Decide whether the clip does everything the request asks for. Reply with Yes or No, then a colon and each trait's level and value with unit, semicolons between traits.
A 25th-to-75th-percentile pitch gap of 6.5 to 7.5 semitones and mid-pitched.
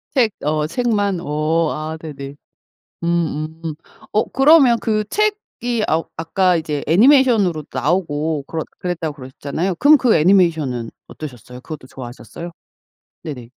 No: wide, 5.6 semitones; medium, 165 Hz